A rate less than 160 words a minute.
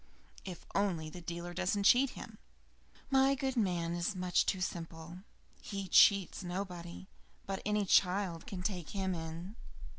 Yes: average, 150 wpm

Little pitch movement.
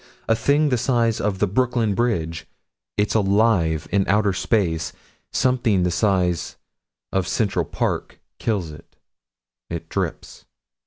No: average, 4.5 semitones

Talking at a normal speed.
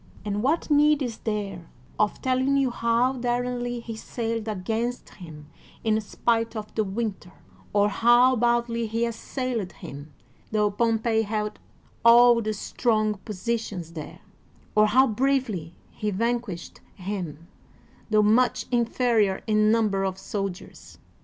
No: slow, 125 wpm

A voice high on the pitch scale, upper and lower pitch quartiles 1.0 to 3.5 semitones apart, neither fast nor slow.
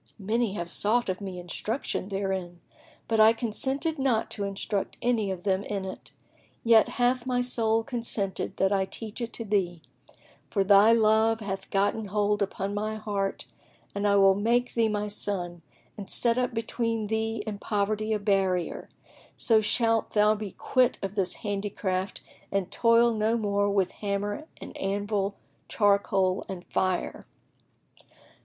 Yes: high, 205 Hz; narrow, 2.5 semitones; average, 155 wpm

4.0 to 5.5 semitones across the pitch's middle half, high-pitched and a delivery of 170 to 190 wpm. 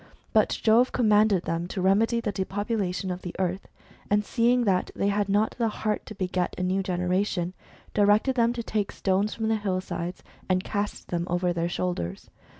No: average, 2.9 semitones; high, 195 Hz; average, 185 wpm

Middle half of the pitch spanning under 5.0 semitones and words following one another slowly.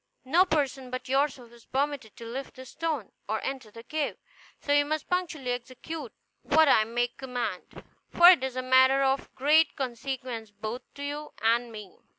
No: average, 3.4 semitones; average, 175 wpm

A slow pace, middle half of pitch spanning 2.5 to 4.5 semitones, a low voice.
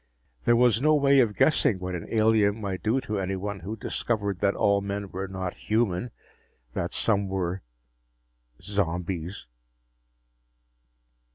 Yes: slow, 130 wpm; average, 2.9 semitones; low, 100 Hz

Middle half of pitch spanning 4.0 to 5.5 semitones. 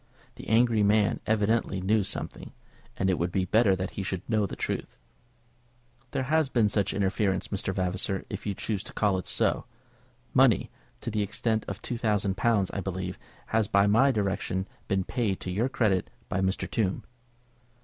No: average, 2.7 semitones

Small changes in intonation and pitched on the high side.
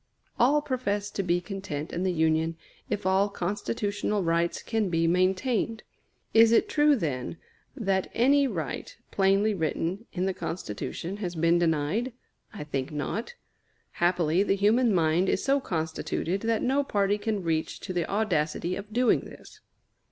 No: average, 4.7 semitones; high, 195 Hz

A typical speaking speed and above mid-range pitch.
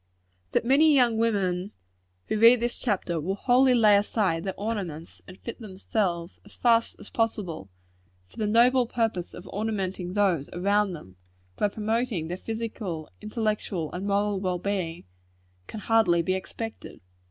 Yes: average, 150 wpm; high, 205 Hz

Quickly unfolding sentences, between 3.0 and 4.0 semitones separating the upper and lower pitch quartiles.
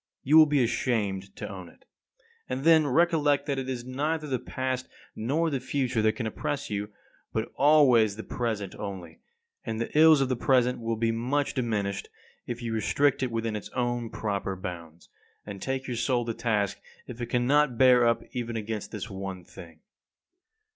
No: average, 180 wpm; average, 3.7 semitones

